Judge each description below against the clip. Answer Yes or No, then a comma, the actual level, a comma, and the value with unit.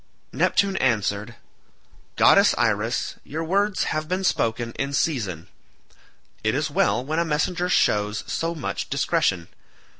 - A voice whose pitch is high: No, medium, 140 Hz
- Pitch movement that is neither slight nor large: No, wide, 7.6 semitones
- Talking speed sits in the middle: No, slow, 125 wpm